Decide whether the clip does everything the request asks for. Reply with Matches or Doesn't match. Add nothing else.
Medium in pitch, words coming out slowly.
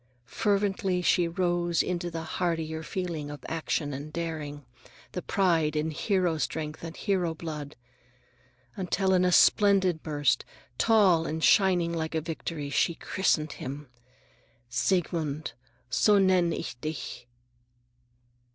Matches